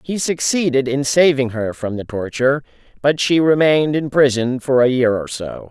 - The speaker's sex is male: Yes, male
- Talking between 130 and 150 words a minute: No, average, 190 wpm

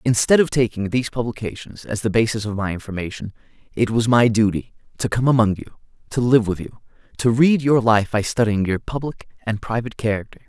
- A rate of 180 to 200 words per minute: Yes, average, 195 wpm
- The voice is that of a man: Yes, male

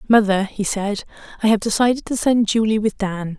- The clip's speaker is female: Yes, female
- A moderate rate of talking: Yes, average, 195 wpm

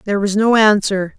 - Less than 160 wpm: No, fast, 205 wpm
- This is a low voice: No, high, 205 Hz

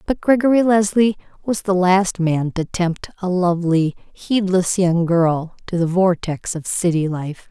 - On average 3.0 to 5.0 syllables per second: Yes, 4.1 syllables/s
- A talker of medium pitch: Yes, medium, 180 Hz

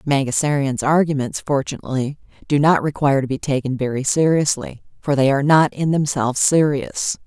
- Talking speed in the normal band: Yes, average, 150 wpm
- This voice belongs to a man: No, female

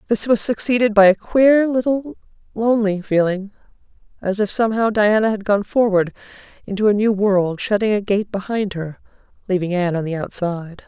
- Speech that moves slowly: No, average, 165 wpm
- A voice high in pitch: Yes, high, 205 Hz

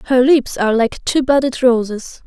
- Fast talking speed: No, average, 185 wpm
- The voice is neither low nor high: No, very high, 250 Hz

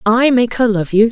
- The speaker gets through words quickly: Yes, fast, 270 wpm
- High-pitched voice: Yes, high, 225 Hz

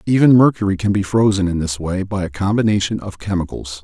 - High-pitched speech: No, low, 100 Hz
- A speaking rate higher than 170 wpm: Yes, fast, 205 wpm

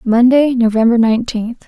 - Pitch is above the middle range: Yes, high, 235 Hz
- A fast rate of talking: No, slow, 105 wpm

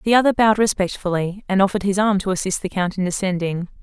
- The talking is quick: Yes, fast, 220 wpm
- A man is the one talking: No, female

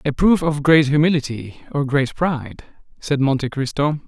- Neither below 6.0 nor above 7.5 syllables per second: No, 4.9 syllables/s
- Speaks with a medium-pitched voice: Yes, medium, 145 Hz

